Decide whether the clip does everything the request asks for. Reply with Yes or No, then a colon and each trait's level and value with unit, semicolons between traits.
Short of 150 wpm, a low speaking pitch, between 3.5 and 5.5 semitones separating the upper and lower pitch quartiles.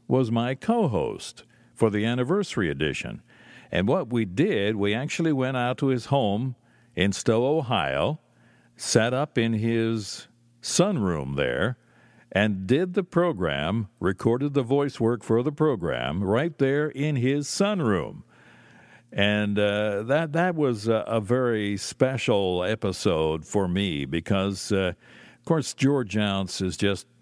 Yes: average, 140 wpm; low, 115 Hz; average, 5.1 semitones